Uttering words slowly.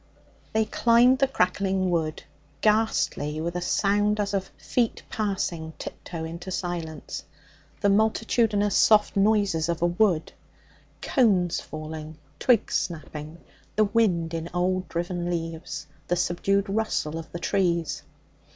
Yes: slow, 125 wpm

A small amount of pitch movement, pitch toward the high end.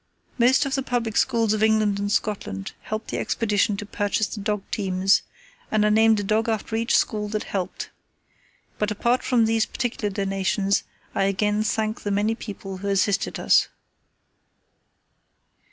Yes: narrow, 1.8 semitones; high, 210 Hz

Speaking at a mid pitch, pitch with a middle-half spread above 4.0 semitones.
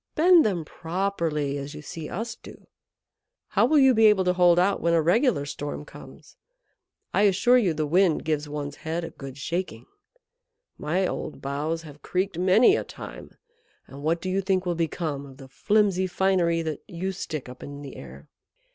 Yes: medium, 170 Hz; average, 4.4 semitones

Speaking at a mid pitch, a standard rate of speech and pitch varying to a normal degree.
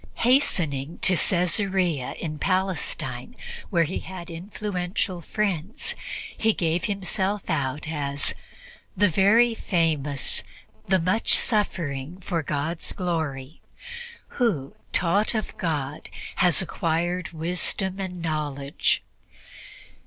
No: medium, 175 Hz; slow, 100 wpm; average, 4.0 semitones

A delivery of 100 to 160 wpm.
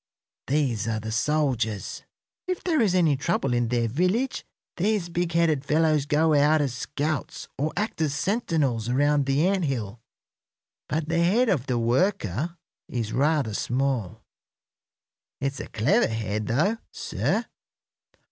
Yes: average, 140 wpm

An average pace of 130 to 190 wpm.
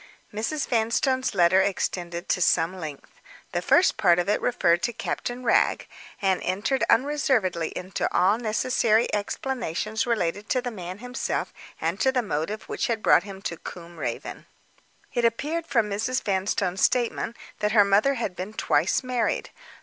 Yes: average, 155 wpm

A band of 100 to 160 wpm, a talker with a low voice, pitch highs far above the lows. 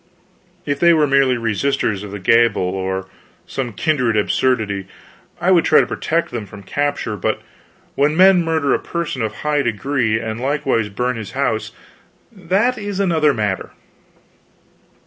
Yes: average, 150 wpm; low, 130 Hz; wide, 6.5 semitones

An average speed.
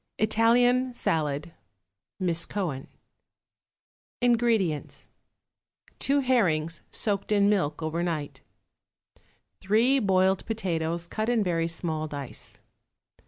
No: slow, 90 wpm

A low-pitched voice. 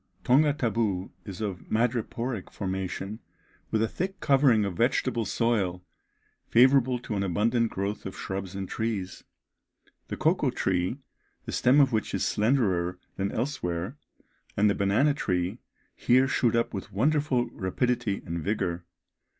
Yes: low, 110 Hz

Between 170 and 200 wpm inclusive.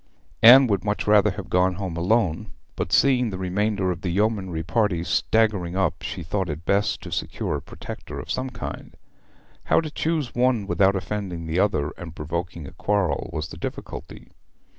Yes: average, 180 wpm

